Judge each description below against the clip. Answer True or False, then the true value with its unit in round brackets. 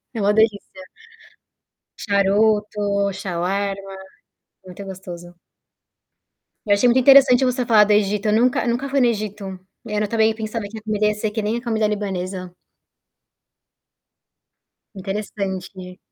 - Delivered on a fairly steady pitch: True (2.3 semitones)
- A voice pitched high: True (210 Hz)